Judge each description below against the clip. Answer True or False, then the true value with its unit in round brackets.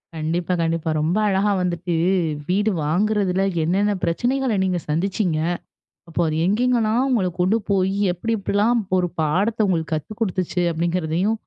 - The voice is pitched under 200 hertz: True (185 Hz)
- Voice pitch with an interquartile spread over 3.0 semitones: True (4.0 semitones)